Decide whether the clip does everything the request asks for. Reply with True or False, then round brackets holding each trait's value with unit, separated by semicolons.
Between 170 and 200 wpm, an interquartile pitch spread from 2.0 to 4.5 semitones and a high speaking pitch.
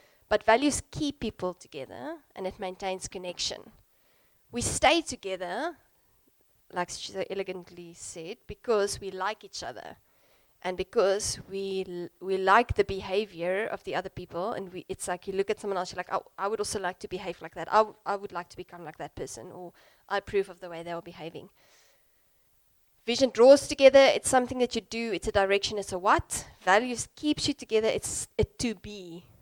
True (195 wpm; 3.4 semitones; 195 Hz)